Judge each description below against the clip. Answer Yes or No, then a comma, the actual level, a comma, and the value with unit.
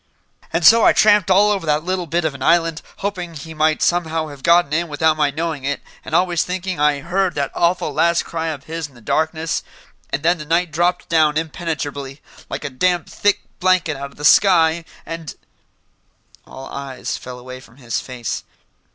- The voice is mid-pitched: Yes, medium, 160 Hz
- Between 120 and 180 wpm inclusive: No, average, 195 wpm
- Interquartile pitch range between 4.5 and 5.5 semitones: No, average, 3.2 semitones